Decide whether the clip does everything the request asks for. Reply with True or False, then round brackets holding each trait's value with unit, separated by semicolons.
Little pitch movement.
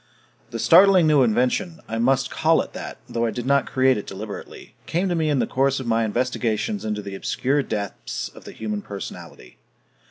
False (5.1 semitones)